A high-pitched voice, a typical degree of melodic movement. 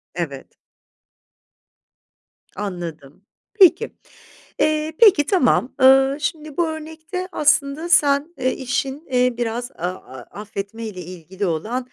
No: very high, 260 Hz; wide, 7.7 semitones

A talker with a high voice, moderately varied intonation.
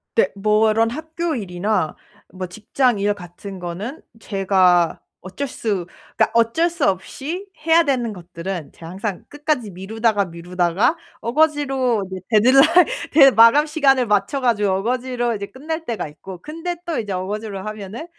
No: high, 220 Hz; wide, 6.2 semitones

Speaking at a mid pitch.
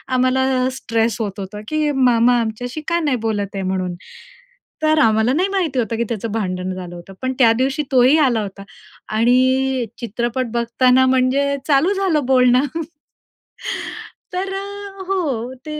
No: very high, 255 Hz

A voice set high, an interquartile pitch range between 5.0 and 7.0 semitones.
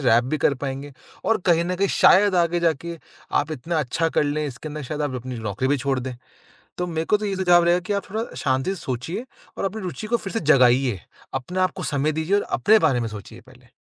No: medium, 155 Hz; wide, 5.6 semitones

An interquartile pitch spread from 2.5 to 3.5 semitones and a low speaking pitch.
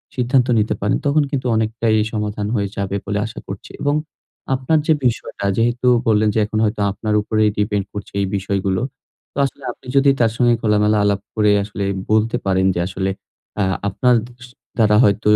Yes: average, 2.8 semitones; low, 105 Hz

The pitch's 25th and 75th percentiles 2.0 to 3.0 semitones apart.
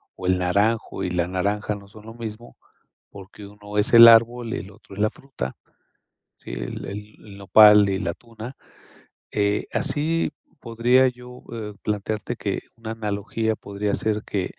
Yes: narrow, 2.5 semitones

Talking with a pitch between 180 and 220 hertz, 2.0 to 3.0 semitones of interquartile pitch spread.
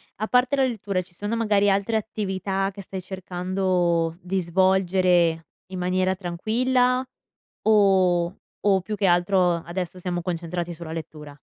Yes: medium, 185 Hz; narrow, 2.5 semitones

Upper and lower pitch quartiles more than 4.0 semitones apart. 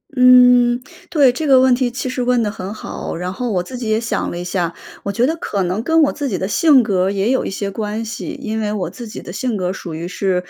Yes: average, 4.7 semitones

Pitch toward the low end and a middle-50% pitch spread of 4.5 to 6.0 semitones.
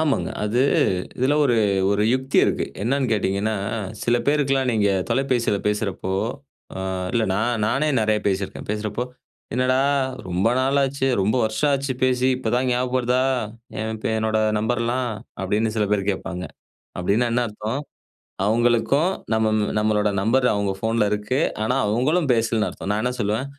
No: low, 115 Hz; average, 3.5 semitones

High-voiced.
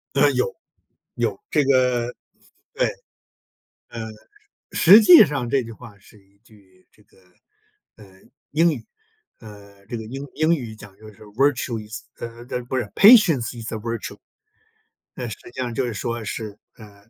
No: low, 120 Hz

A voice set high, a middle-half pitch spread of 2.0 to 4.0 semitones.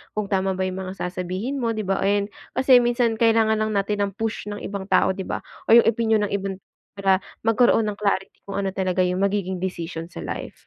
Yes: high, 200 Hz; average, 2.7 semitones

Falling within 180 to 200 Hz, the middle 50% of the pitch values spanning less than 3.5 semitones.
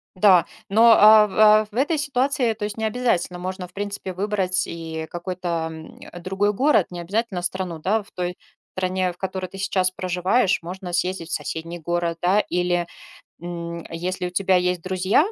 Yes: medium, 185 Hz; average, 2.8 semitones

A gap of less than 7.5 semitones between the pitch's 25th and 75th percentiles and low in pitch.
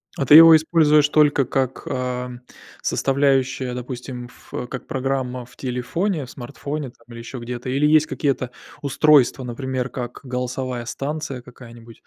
Yes: narrow, 2.6 semitones; low, 130 Hz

